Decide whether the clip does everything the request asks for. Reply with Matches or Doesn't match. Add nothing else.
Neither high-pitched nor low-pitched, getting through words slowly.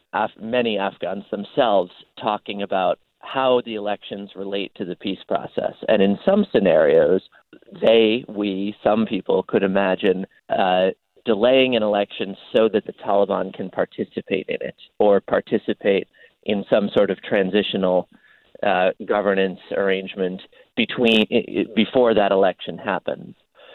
Doesn't match